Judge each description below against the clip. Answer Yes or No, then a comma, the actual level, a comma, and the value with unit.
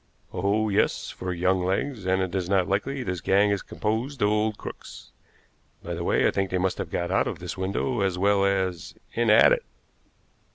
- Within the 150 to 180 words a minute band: No, fast, 205 wpm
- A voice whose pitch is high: No, low, 100 Hz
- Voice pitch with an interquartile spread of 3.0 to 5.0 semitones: No, narrow, 2.4 semitones